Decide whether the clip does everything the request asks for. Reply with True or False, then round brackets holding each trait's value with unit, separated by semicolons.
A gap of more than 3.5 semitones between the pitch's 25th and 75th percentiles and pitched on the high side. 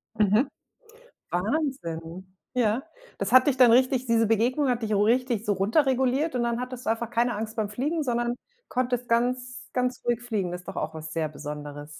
True (3.9 semitones; 235 Hz)